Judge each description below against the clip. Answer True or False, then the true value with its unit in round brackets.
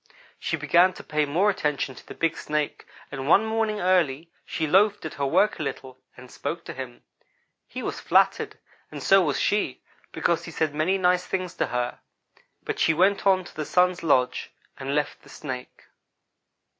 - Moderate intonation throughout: True (4.7 semitones)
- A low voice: False (160 Hz)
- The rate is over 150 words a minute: True (185 wpm)